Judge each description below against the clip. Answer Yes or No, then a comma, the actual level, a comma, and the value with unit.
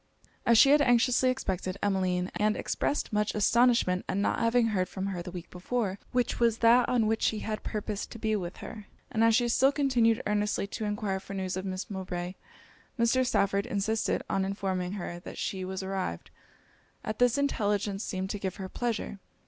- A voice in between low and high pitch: No, high, 210 Hz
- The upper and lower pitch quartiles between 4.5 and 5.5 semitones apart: No, average, 3.4 semitones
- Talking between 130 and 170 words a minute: No, average, 190 wpm